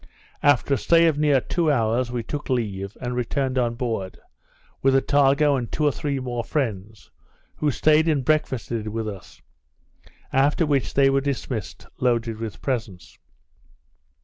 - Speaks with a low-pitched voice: Yes, low, 130 Hz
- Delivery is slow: No, average, 150 wpm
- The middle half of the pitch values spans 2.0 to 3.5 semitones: No, average, 4.0 semitones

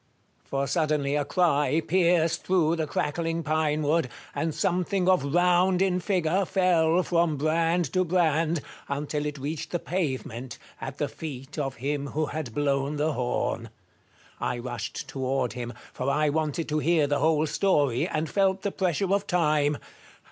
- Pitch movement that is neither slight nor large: Yes, average, 3.4 semitones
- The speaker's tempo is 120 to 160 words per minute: Yes, average, 155 wpm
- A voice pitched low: No, medium, 155 Hz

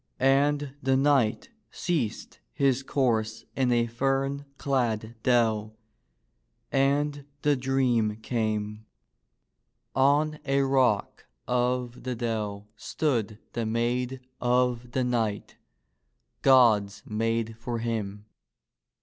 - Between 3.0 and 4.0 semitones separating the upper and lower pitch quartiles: Yes, average, 3.4 semitones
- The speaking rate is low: Yes, slow, 100 wpm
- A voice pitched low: Yes, low, 120 Hz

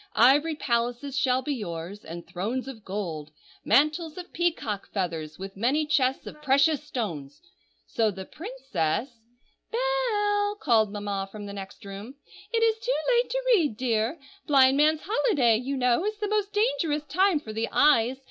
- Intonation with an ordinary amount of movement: No, wide, 8.4 semitones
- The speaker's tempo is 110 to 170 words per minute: Yes, average, 155 wpm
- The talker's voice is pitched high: Yes, very high, 265 Hz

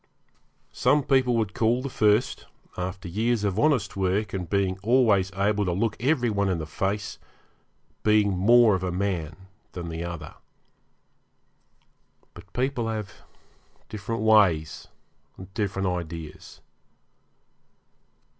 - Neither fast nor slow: No, slow, 125 wpm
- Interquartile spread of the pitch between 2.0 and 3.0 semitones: No, average, 3.5 semitones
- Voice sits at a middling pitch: No, low, 100 Hz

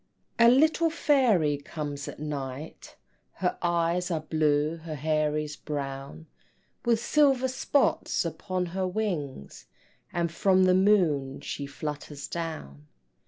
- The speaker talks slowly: Yes, slow, 120 wpm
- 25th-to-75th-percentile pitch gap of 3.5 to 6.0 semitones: Yes, average, 4.5 semitones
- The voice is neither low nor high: Yes, medium, 160 Hz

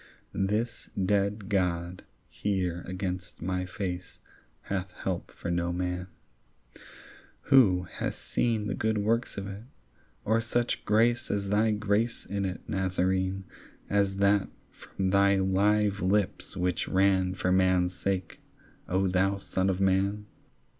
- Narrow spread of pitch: Yes, narrow, 1.9 semitones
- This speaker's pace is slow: Yes, slow, 130 wpm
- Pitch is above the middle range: No, very low, 95 Hz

